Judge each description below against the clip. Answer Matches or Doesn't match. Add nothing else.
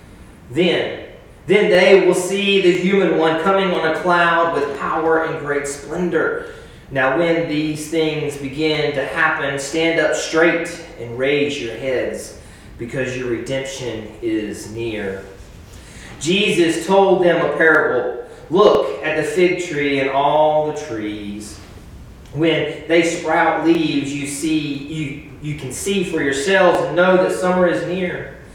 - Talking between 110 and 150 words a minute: Matches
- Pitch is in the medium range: Matches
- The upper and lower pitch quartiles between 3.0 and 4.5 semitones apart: Matches